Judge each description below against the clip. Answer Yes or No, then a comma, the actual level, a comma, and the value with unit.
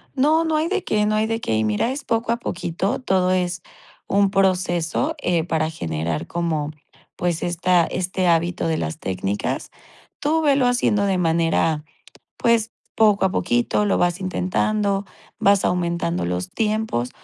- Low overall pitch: No, medium, 185 Hz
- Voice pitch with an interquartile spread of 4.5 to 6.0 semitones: Yes, average, 4.8 semitones